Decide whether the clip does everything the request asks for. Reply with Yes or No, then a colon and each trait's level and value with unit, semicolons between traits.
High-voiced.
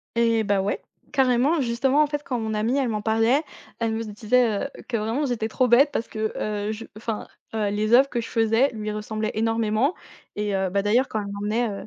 Yes: high, 225 Hz